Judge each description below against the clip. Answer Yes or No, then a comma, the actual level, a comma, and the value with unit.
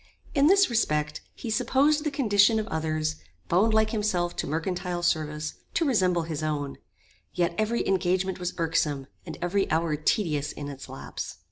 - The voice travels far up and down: Yes, wide, 5.7 semitones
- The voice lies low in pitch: No, medium, 175 Hz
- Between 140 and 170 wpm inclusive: Yes, average, 160 wpm